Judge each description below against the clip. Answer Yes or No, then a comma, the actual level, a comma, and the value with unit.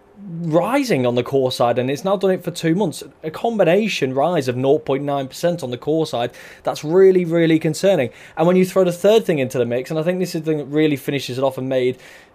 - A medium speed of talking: No, fast, 245 wpm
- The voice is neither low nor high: Yes, medium, 155 Hz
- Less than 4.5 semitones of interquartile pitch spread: No, average, 5.3 semitones